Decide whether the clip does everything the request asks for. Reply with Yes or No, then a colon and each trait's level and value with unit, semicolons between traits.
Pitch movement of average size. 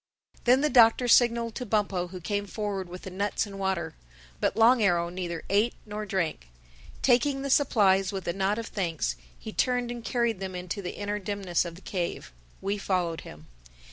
Yes: average, 3.9 semitones